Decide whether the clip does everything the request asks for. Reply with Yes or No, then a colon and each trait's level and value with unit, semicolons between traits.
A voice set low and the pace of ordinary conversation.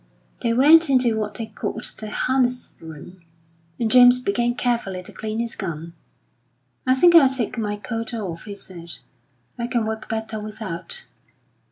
No: high, 225 Hz; average, 160 wpm